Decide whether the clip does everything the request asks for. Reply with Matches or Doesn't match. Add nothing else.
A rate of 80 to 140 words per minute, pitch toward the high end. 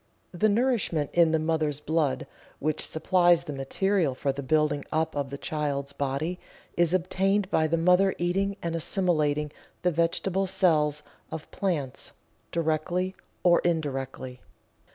Doesn't match